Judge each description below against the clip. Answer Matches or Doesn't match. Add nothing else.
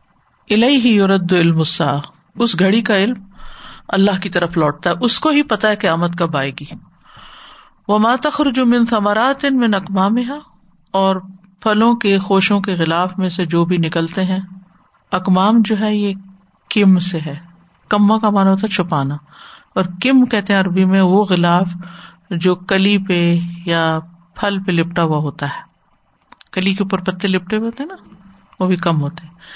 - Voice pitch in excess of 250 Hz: Doesn't match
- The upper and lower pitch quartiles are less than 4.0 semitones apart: Matches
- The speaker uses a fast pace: Doesn't match